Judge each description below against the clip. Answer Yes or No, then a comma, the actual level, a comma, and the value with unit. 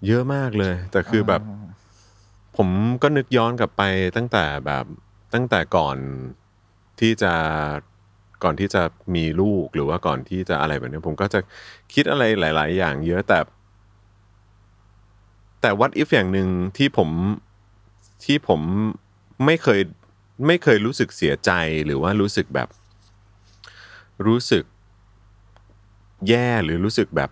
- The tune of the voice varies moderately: No, narrow, 1.5 semitones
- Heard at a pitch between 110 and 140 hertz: No, low, 100 Hz